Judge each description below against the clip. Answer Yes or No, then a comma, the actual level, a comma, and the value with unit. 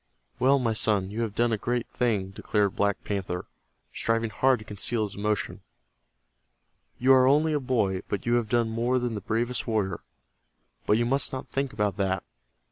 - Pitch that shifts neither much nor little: Yes, average, 3.3 semitones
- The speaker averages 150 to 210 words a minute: Yes, average, 185 wpm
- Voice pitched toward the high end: No, low, 115 Hz